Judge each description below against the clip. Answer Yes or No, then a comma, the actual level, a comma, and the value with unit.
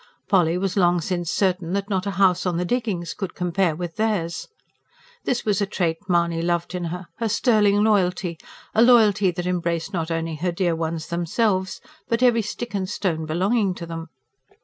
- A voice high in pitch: No, medium, 180 Hz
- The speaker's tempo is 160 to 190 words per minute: Yes, average, 185 wpm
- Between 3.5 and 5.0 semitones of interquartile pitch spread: No, average, 3.1 semitones